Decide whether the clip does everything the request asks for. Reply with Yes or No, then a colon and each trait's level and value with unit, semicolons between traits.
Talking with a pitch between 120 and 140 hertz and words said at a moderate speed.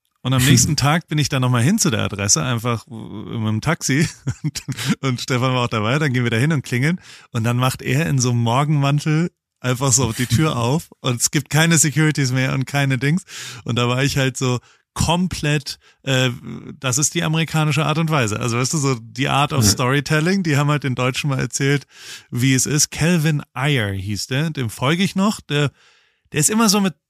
No: low, 135 Hz; fast, 215 wpm